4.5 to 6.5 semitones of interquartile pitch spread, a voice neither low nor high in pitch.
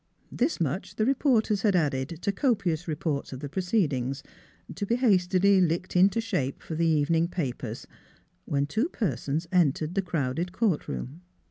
Yes: wide, 5.5 semitones; medium, 175 Hz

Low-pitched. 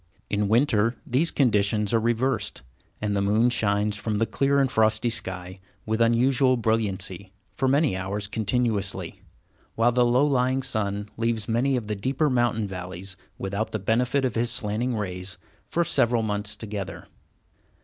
Yes: low, 110 Hz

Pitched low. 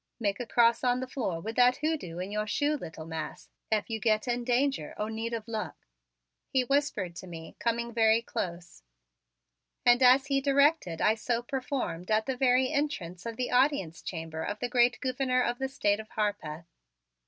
No: high, 235 Hz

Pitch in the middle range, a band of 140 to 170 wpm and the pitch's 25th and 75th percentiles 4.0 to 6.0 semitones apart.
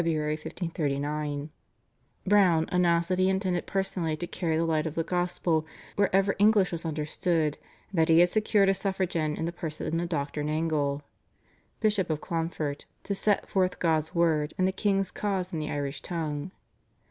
No: medium, 165 Hz; average, 165 wpm; average, 3.4 semitones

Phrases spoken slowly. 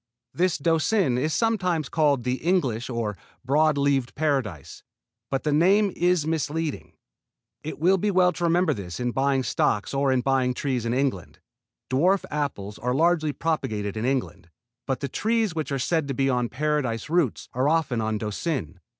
No: average, 170 wpm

